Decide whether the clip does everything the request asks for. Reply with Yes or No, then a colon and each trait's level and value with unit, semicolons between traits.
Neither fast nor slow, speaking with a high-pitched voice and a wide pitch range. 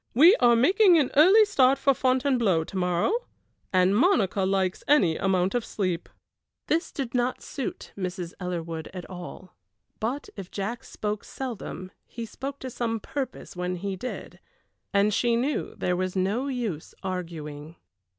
Yes: average, 150 wpm; high, 205 Hz; wide, 6.1 semitones